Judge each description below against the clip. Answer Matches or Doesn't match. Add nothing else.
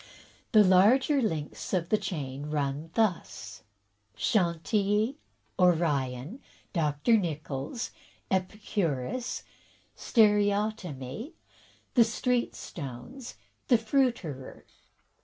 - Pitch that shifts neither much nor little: Doesn't match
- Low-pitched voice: Doesn't match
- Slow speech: Matches